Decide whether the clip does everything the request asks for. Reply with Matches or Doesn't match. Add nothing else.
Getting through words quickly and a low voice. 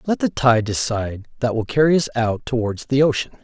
Matches